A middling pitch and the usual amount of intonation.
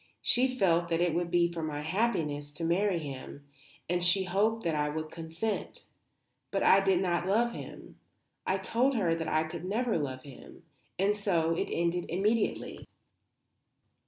Yes: medium, 175 Hz; average, 3.8 semitones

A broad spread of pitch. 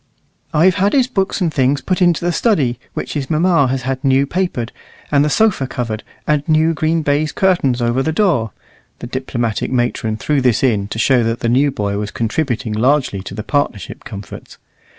No: average, 5.0 semitones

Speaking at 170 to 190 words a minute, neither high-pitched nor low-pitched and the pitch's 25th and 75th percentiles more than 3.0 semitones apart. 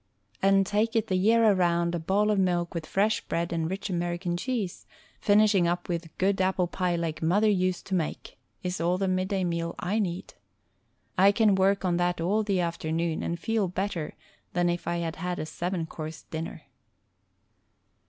No: average, 185 wpm; medium, 180 Hz; narrow, 2.4 semitones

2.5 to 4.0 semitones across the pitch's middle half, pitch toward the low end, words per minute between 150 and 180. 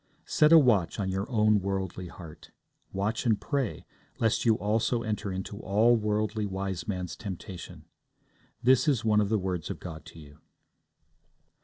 Yes: average, 3.1 semitones; low, 105 Hz; average, 155 wpm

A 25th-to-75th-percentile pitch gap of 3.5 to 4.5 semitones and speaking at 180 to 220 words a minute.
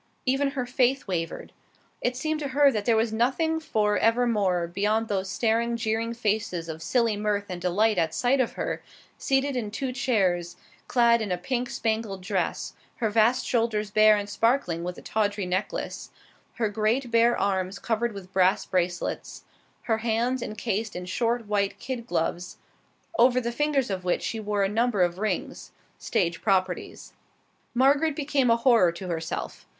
No: average, 4.0 semitones; average, 165 wpm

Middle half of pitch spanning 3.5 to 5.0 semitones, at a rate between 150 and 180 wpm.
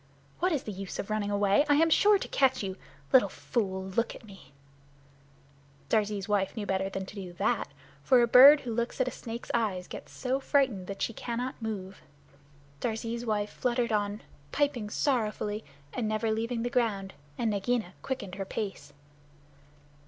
Yes: average, 3.8 semitones; average, 175 wpm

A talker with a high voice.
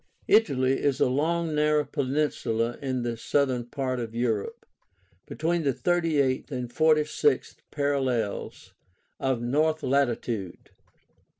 No: low, 135 Hz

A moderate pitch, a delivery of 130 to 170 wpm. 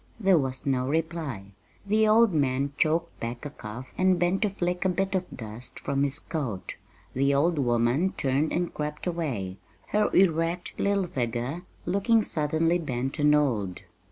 Yes: medium, 150 Hz; average, 160 wpm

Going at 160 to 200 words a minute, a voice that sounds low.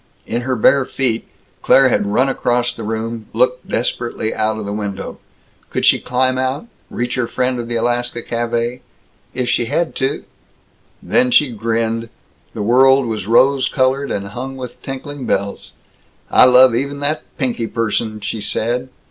Yes: average, 165 wpm; low, 120 Hz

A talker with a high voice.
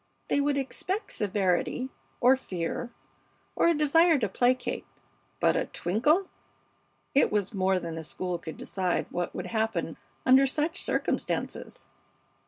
Yes: high, 225 Hz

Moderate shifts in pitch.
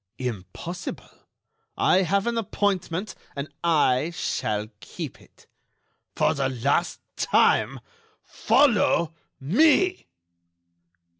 No: wide, 7.1 semitones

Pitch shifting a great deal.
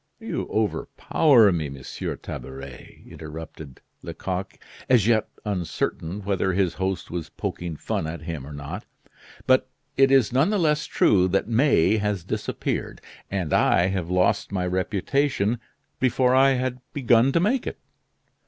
Yes: wide, 6.9 semitones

